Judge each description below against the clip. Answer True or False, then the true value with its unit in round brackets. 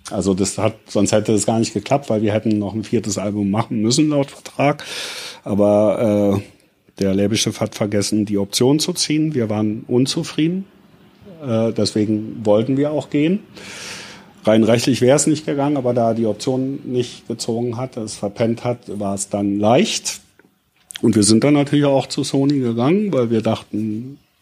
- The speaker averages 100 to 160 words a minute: False (175 wpm)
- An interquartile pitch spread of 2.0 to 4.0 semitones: False (4.6 semitones)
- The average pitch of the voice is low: True (115 Hz)